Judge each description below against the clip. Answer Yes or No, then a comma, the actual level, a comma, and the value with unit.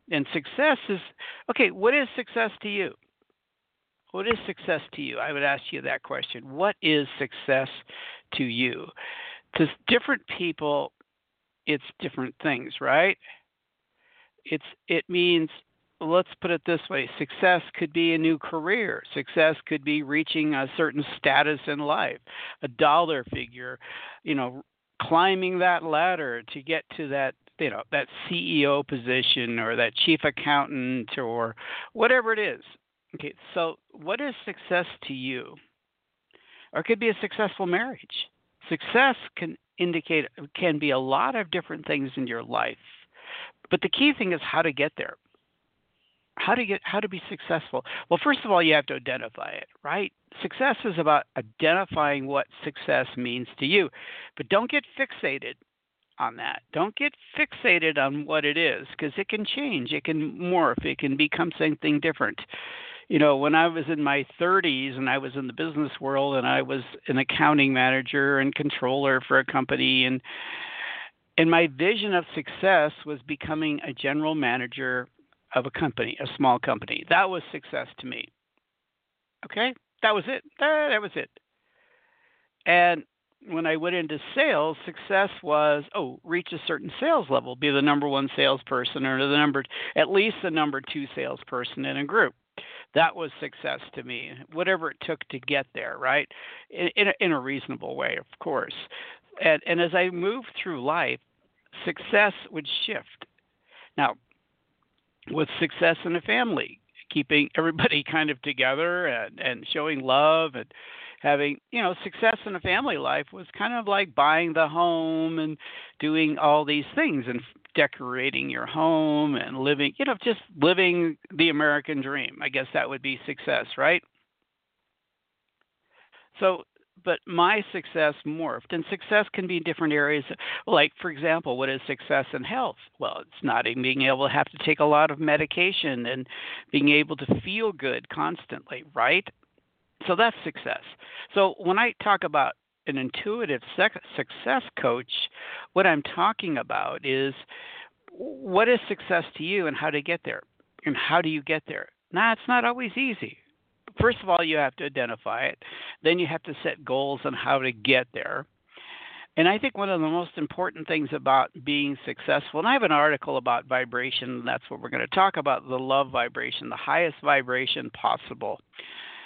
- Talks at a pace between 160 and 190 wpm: Yes, average, 170 wpm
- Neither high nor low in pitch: Yes, medium, 160 Hz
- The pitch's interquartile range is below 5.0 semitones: No, wide, 5.5 semitones